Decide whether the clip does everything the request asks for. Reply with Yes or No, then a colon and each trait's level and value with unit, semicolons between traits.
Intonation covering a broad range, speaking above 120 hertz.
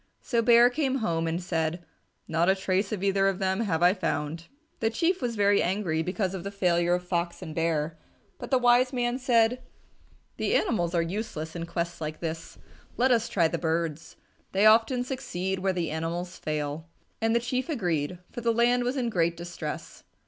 Yes: wide, 5.7 semitones; medium, 185 Hz